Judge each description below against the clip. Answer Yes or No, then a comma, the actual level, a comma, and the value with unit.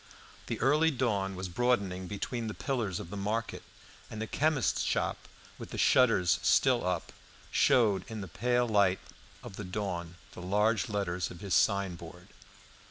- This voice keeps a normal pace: Yes, average, 160 wpm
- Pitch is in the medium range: No, low, 100 Hz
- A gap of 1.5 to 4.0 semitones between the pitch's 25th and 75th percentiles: No, average, 4.4 semitones